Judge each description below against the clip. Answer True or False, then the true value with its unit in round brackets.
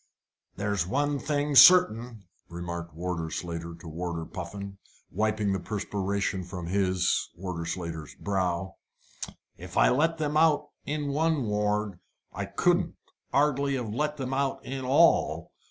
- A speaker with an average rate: False (130 wpm)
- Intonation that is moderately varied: False (7.9 semitones)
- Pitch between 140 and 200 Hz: False (100 Hz)